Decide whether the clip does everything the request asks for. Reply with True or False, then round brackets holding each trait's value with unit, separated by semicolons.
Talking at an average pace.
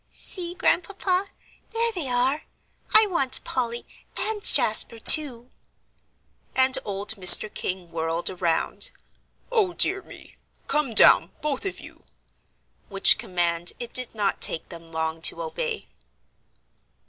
False (125 wpm)